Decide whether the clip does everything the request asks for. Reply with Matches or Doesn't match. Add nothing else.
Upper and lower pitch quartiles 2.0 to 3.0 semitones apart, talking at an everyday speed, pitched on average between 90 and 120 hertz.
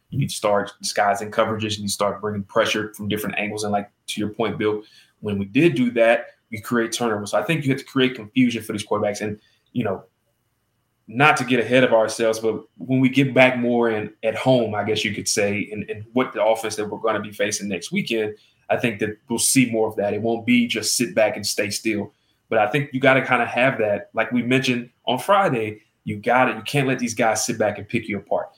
Doesn't match